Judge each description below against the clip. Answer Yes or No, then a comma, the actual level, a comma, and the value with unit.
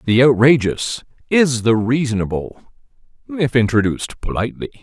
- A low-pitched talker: Yes, low, 125 Hz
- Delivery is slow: Yes, slow, 100 wpm